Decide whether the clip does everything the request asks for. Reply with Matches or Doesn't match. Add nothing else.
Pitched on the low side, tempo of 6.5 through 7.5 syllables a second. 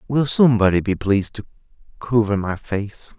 Doesn't match